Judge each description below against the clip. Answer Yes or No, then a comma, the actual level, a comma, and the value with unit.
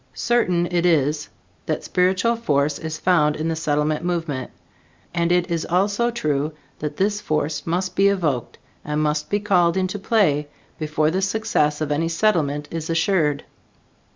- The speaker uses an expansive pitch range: No, average, 3.8 semitones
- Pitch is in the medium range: Yes, medium, 165 Hz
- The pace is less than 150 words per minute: No, average, 155 wpm